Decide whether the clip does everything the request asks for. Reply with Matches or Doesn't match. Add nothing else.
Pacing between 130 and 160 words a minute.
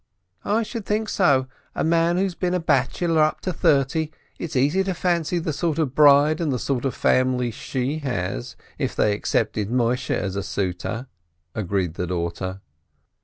Doesn't match